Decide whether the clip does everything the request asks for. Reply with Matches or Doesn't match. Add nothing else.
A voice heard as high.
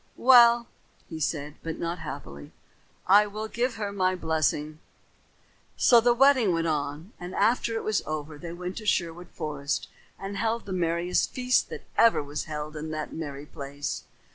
Doesn't match